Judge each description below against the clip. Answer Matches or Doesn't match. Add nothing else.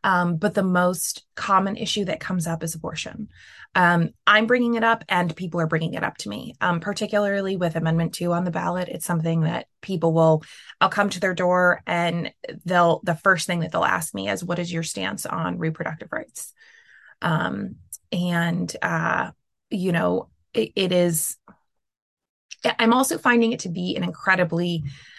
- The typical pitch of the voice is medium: Matches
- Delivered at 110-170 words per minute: Doesn't match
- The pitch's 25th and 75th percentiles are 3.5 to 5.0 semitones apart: Doesn't match